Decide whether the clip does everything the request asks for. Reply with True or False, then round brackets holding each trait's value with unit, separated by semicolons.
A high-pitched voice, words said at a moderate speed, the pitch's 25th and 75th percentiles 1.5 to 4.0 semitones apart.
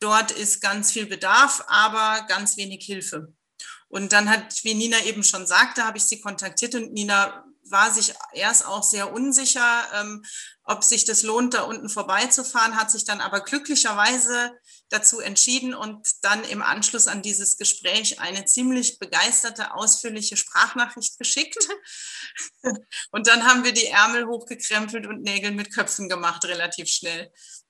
True (220 Hz; 155 wpm; 2.8 semitones)